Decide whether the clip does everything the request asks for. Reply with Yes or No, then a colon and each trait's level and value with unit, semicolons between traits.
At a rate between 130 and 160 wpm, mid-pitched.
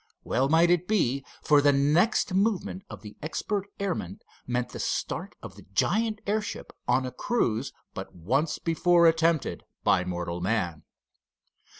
Yes: average, 150 wpm; medium, 150 Hz